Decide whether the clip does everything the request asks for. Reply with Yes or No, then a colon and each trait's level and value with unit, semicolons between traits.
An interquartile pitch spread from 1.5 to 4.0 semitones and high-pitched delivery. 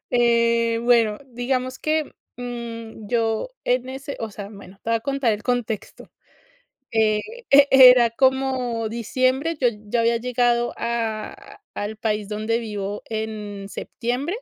Yes: narrow, 2.5 semitones; high, 235 Hz